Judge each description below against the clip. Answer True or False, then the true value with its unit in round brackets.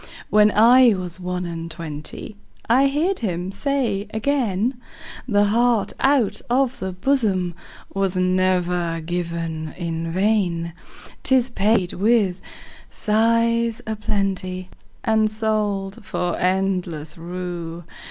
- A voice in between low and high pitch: False (195 Hz)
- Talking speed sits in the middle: False (95 wpm)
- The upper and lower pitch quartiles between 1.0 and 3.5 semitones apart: False (4.1 semitones)